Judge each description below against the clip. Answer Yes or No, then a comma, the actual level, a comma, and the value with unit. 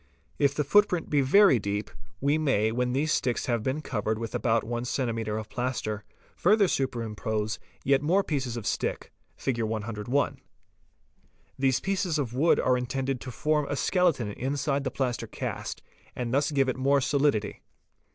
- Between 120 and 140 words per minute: No, average, 170 wpm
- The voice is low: Yes, low, 130 Hz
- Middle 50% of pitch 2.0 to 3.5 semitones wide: No, average, 4.0 semitones